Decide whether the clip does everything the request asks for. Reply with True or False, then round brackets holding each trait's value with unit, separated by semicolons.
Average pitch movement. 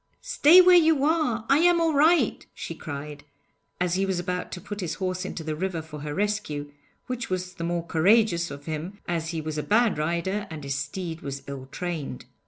False (5.8 semitones)